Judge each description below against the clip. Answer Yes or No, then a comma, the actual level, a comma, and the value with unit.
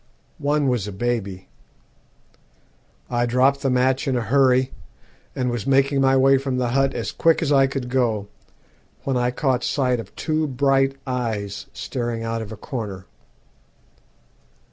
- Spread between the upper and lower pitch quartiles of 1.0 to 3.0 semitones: Yes, narrow, 2.4 semitones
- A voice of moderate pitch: No, low, 125 Hz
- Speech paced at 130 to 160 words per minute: Yes, average, 155 wpm